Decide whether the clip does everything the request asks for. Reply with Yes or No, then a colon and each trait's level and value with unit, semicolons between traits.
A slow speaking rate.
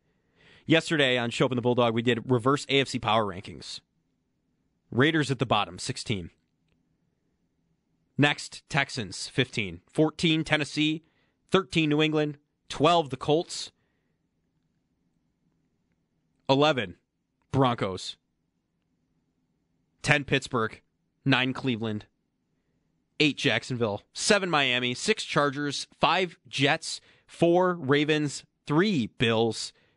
Yes: slow, 90 wpm